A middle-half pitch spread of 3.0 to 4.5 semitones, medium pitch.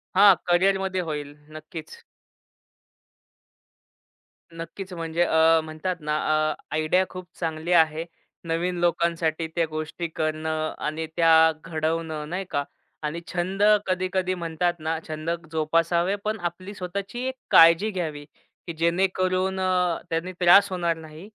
No: narrow, 2.6 semitones; medium, 170 Hz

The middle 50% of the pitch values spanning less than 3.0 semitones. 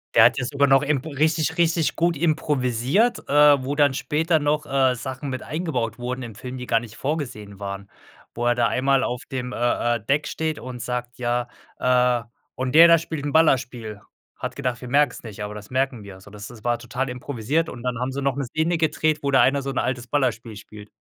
No: average, 3.5 semitones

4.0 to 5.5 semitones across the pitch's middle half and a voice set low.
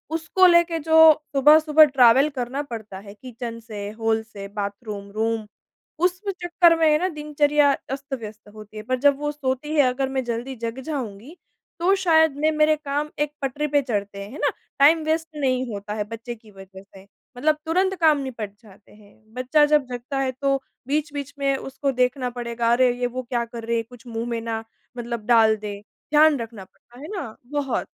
No: average, 4.9 semitones; very high, 255 Hz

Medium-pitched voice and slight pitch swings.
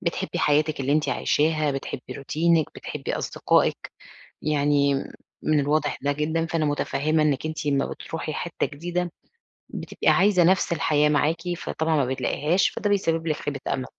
Yes: medium, 155 Hz; narrow, 2.1 semitones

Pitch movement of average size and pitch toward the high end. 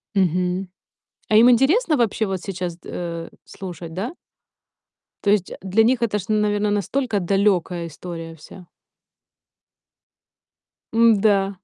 Yes: average, 3.4 semitones; high, 195 Hz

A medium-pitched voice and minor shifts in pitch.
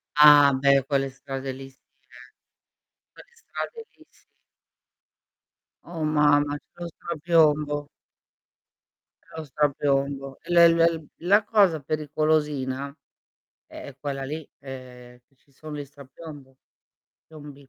Yes: medium, 145 Hz; narrow, 2.3 semitones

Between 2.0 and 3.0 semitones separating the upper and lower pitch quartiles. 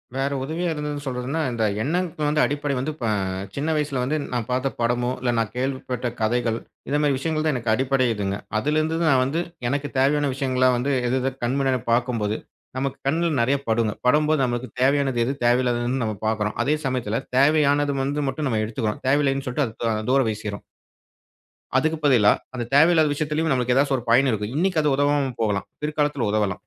No: average, 3.5 semitones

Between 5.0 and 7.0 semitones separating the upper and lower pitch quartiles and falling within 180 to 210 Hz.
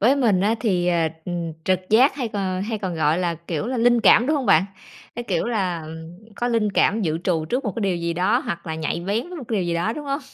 Yes: wide, 5.5 semitones; high, 190 Hz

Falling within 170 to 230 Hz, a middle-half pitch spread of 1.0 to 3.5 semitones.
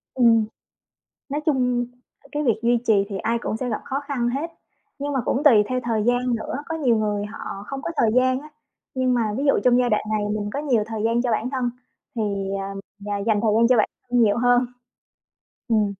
No: high, 240 Hz; average, 2.8 semitones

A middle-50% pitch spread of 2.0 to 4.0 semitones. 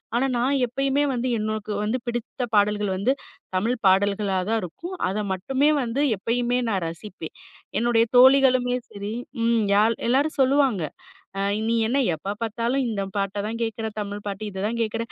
Yes: average, 3.6 semitones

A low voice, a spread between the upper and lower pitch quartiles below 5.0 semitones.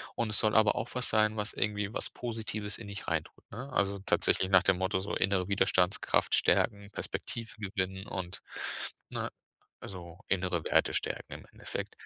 Yes: low, 100 Hz; narrow, 2.4 semitones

